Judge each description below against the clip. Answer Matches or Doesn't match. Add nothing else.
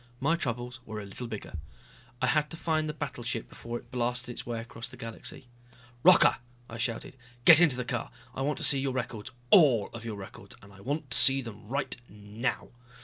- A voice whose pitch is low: Matches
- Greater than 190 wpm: Matches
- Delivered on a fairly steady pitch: Doesn't match